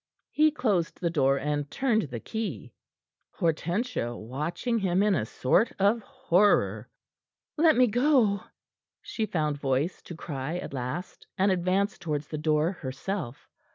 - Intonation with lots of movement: Yes, wide, 6.6 semitones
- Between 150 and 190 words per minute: No, average, 140 wpm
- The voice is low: No, medium, 175 Hz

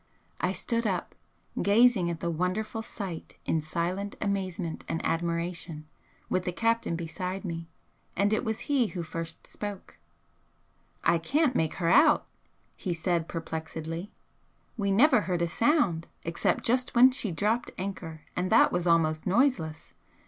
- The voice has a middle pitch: Yes, medium, 180 Hz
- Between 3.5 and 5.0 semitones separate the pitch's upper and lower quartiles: Yes, average, 4.6 semitones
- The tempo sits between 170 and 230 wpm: No, average, 145 wpm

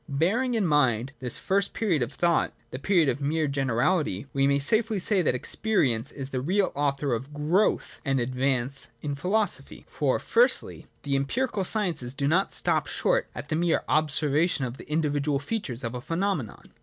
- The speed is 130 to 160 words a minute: No, average, 175 wpm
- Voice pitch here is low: No, medium, 145 Hz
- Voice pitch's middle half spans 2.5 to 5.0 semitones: No, wide, 5.5 semitones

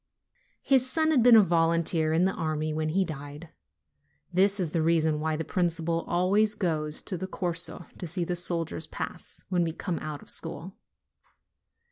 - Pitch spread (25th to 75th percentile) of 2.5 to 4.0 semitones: Yes, average, 2.9 semitones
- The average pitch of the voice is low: No, medium, 170 Hz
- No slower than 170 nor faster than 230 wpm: Yes, average, 175 wpm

